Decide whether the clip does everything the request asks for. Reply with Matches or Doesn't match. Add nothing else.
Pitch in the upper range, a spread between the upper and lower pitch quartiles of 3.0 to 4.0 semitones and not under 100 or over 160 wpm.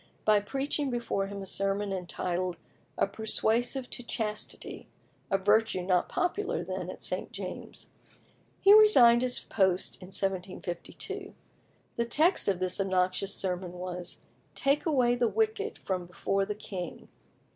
Doesn't match